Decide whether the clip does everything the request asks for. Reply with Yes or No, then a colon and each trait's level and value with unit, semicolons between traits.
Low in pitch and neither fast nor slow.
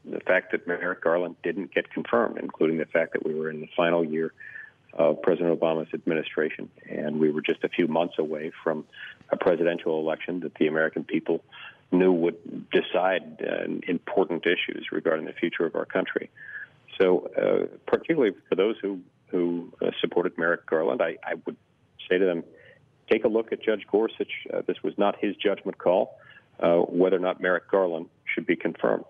Yes: very low, 95 Hz; average, 180 wpm